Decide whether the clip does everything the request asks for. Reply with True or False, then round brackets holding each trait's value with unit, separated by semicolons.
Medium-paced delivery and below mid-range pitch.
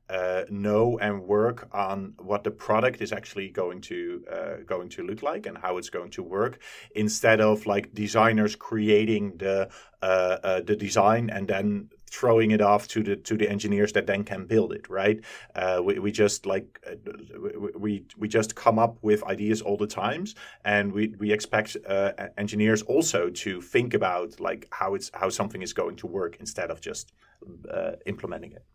True (190 wpm; 105 Hz)